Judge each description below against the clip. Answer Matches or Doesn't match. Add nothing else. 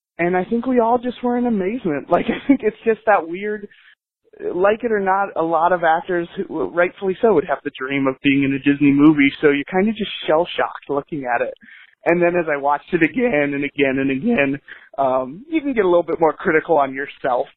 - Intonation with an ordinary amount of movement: Doesn't match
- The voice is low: Doesn't match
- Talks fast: Matches